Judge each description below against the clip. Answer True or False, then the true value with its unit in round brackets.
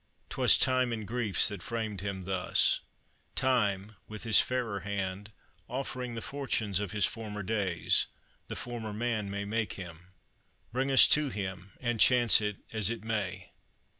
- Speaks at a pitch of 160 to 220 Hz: False (105 Hz)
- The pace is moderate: True (155 wpm)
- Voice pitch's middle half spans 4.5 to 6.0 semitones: False (3.2 semitones)